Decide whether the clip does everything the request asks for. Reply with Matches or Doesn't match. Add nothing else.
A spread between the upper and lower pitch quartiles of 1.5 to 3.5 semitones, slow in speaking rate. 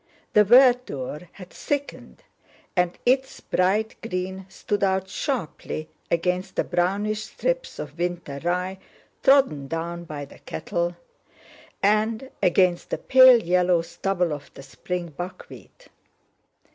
Doesn't match